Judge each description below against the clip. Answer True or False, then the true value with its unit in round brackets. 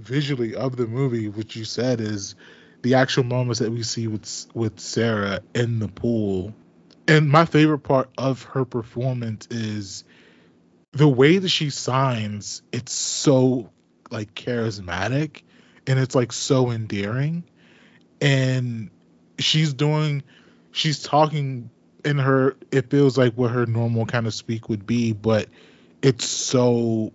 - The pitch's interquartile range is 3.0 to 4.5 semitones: True (3.6 semitones)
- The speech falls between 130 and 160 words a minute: True (140 wpm)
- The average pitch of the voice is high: False (120 Hz)